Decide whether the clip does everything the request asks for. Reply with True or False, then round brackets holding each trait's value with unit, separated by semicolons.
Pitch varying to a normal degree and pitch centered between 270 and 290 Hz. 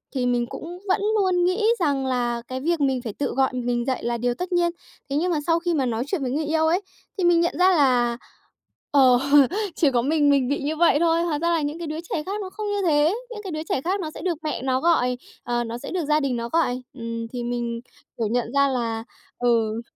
False (5.7 semitones; 285 Hz)